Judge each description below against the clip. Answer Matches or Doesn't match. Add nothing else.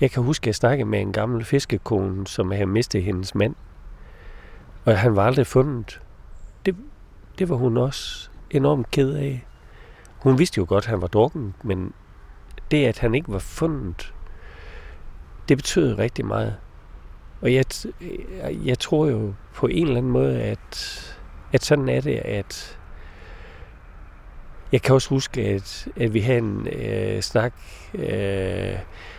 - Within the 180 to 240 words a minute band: Doesn't match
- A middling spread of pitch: Doesn't match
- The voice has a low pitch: Matches